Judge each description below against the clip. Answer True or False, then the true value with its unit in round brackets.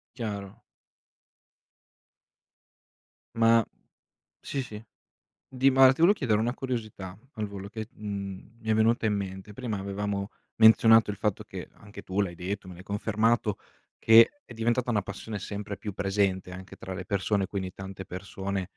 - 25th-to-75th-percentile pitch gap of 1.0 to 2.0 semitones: False (2.6 semitones)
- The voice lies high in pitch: False (105 Hz)